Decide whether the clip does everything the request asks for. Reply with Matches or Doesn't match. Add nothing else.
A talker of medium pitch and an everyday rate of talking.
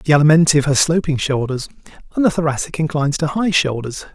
Matches